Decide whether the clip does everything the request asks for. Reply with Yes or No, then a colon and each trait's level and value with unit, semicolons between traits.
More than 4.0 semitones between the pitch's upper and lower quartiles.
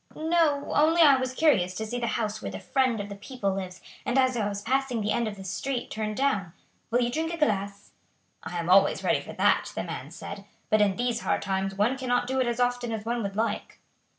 Yes: average, 4.4 semitones